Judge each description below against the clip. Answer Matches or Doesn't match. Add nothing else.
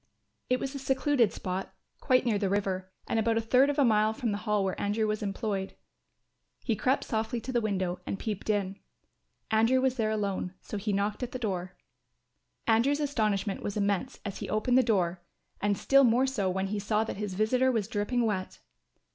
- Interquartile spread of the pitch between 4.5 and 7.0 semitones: Doesn't match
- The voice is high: Matches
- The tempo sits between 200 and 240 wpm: Matches